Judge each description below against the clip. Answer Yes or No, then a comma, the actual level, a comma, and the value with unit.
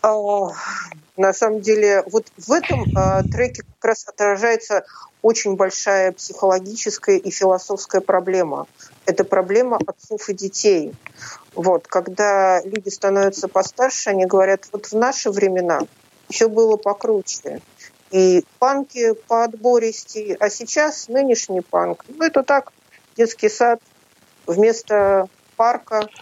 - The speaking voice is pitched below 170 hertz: No, high, 210 Hz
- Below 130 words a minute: Yes, average, 120 wpm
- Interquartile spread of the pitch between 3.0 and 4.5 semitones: Yes, average, 3.4 semitones